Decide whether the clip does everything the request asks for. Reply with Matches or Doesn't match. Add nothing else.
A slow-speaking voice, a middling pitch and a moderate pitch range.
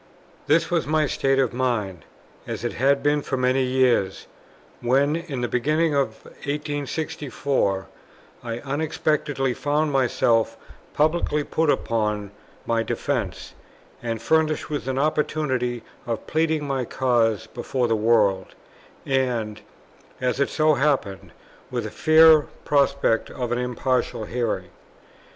Doesn't match